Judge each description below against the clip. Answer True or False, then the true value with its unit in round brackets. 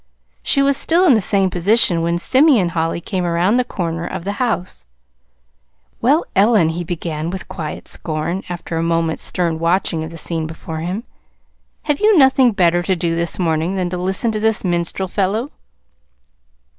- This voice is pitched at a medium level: True (180 Hz)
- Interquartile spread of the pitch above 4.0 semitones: True (4.5 semitones)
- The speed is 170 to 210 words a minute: True (175 wpm)